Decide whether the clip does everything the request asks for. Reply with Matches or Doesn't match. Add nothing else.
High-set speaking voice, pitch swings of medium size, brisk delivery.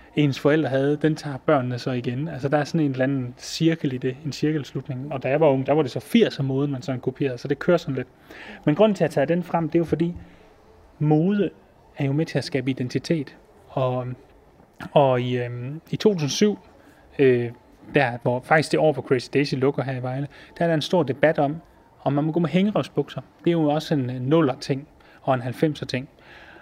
Doesn't match